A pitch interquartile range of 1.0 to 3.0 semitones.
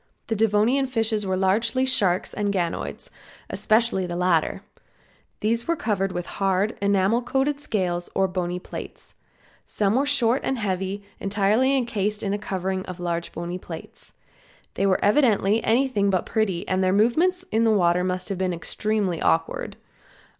No: average, 3.5 semitones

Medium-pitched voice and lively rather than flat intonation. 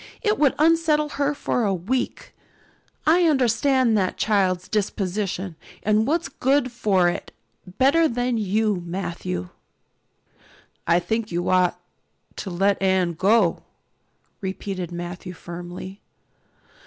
No: high, 200 Hz; wide, 6.2 semitones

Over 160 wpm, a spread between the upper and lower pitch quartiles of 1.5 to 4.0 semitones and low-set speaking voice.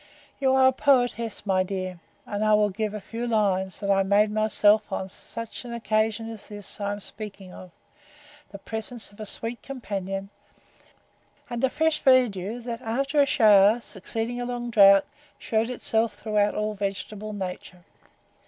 No: average, 170 wpm; average, 2.9 semitones; high, 215 Hz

